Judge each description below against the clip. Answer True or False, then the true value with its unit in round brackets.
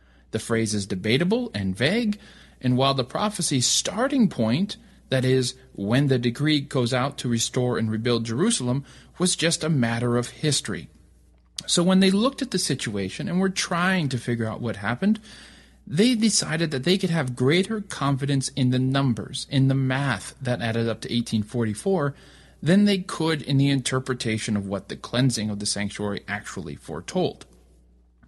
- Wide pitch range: True (6.1 semitones)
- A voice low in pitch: True (130 Hz)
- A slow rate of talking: False (170 wpm)